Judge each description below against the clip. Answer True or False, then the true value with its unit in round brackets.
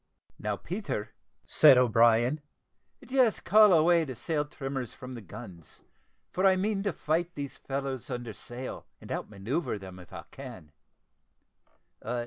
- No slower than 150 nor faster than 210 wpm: False (140 wpm)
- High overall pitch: False (135 Hz)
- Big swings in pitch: True (6.7 semitones)